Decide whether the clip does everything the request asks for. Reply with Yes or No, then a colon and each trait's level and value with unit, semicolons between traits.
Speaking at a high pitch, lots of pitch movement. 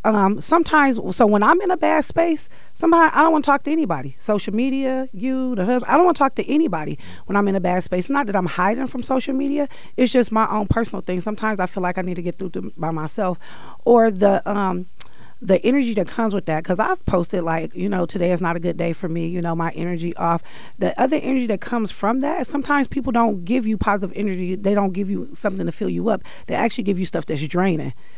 Yes: high, 210 Hz; wide, 6.3 semitones